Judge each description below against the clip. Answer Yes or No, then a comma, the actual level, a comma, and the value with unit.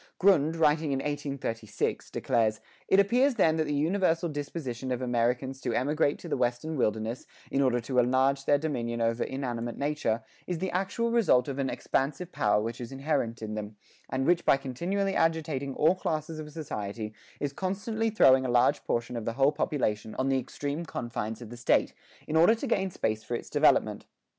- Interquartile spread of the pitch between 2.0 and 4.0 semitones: No, average, 5.1 semitones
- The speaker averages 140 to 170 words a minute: No, average, 185 wpm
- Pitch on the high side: No, low, 135 Hz